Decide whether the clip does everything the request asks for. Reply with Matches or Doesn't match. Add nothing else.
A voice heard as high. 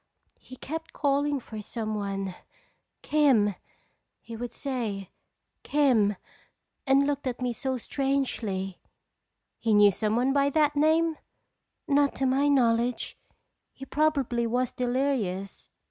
Matches